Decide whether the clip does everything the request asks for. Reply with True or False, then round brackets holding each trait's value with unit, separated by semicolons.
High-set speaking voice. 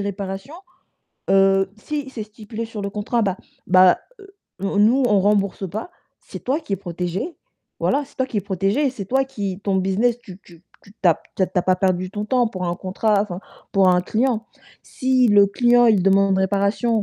True (200 Hz)